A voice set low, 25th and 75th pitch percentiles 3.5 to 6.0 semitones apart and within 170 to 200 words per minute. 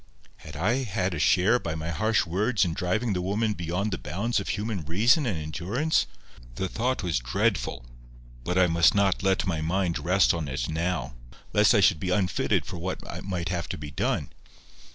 Yes: very low, 90 Hz; average, 3.8 semitones; average, 195 wpm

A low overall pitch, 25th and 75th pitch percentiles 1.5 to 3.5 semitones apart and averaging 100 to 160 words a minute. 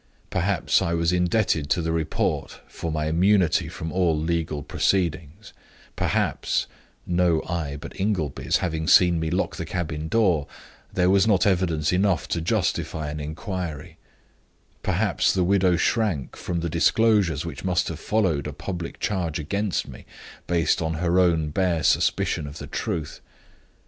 Yes: very low, 85 Hz; average, 2.9 semitones; average, 150 wpm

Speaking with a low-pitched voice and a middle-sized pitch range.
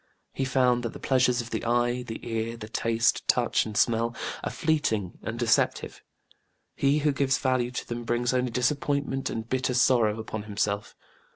No: low, 120 Hz; narrow, 2.3 semitones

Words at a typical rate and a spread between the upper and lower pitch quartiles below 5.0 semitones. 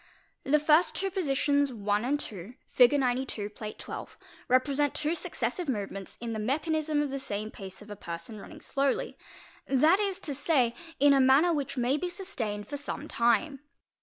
No: average, 165 wpm; wide, 5.4 semitones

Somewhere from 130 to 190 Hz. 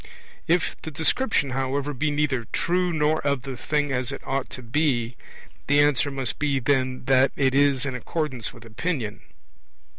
Yes: medium, 140 Hz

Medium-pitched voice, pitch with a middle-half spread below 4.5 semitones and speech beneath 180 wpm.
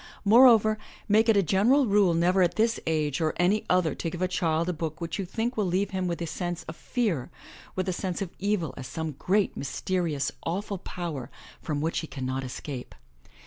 No: medium, 180 Hz; average, 4.1 semitones; fast, 205 wpm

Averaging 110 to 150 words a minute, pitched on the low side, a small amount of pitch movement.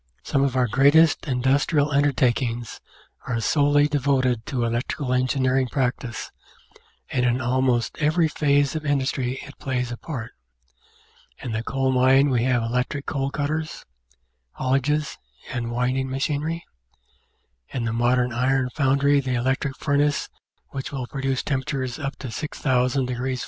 Yes: average, 140 wpm; low, 130 Hz; narrow, 2.3 semitones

